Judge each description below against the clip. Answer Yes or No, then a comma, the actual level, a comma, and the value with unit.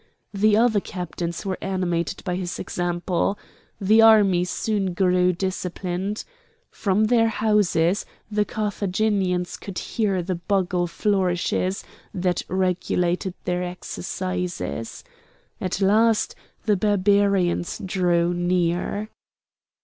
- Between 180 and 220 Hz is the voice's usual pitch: Yes, medium, 185 Hz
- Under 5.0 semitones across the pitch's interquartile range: Yes, narrow, 2.5 semitones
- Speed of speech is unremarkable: No, slow, 100 wpm